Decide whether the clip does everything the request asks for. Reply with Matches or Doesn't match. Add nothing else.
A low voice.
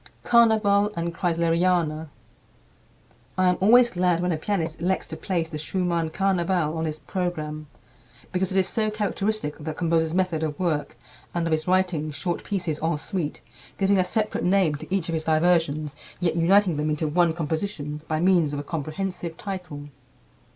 Doesn't match